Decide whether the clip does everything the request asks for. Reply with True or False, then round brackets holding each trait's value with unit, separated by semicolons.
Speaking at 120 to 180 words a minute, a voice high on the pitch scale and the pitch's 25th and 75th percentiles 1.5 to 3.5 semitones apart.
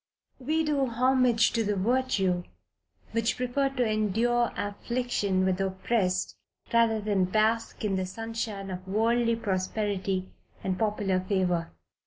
False (135 wpm; 215 Hz; 3.9 semitones)